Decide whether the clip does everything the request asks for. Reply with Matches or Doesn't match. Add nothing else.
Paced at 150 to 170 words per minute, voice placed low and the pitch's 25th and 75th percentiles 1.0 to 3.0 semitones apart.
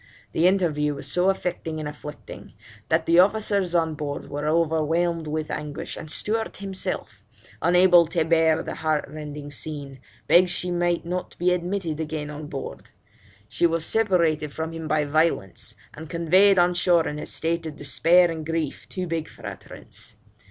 Doesn't match